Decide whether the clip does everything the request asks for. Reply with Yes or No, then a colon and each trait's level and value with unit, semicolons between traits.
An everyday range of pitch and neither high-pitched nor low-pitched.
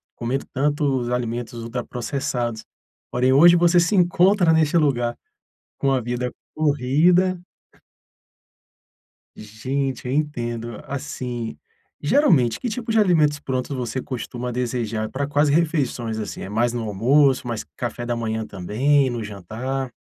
No: average, 3.8 semitones; low, 130 Hz